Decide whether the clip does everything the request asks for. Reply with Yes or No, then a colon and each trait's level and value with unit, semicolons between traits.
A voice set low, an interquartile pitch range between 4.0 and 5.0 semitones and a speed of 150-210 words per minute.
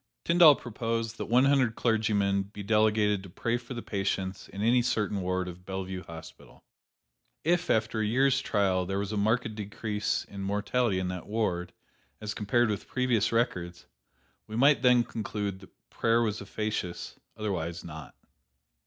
No: low, 105 Hz; average, 3.2 semitones; average, 160 wpm